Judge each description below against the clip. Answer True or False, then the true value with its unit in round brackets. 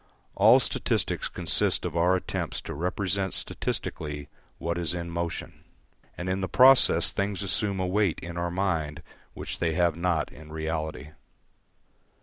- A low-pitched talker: True (85 Hz)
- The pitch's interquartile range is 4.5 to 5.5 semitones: False (2.8 semitones)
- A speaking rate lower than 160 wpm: True (145 wpm)